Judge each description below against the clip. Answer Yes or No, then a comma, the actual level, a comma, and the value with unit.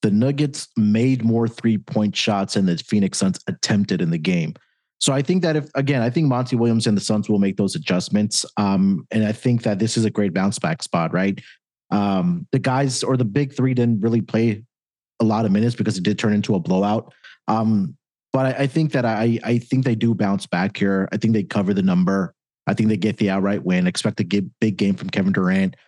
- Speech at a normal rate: No, fast, 230 wpm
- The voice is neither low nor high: No, low, 115 Hz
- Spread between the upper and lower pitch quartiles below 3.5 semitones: No, average, 4.3 semitones